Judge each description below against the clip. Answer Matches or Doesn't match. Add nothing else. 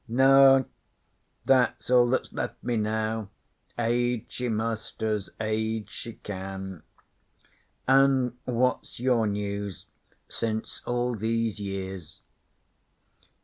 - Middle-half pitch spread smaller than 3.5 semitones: Matches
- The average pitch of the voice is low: Matches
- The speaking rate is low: Matches